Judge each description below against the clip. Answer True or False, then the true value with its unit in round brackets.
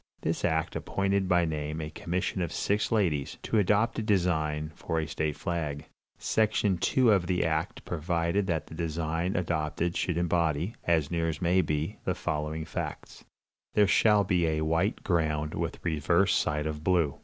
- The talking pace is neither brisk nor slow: True (170 wpm)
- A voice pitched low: True (85 Hz)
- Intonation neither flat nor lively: True (3.0 semitones)